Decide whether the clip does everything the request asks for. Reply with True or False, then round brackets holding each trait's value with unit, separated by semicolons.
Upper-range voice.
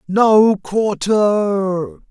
True (195 Hz)